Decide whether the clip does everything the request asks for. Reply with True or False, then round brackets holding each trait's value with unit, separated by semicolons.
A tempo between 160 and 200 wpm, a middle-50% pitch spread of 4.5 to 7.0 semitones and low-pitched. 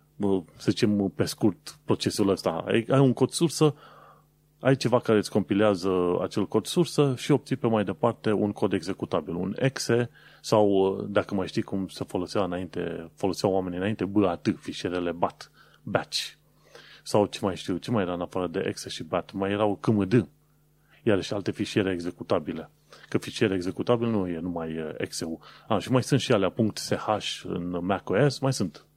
True (170 wpm; 4.8 semitones; 105 Hz)